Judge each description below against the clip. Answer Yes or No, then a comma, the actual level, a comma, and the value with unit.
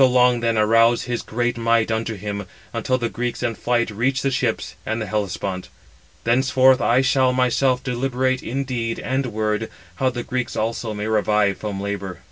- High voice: No, low, 120 Hz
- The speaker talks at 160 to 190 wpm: Yes, average, 180 wpm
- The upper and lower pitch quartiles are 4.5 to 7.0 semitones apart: No, average, 2.9 semitones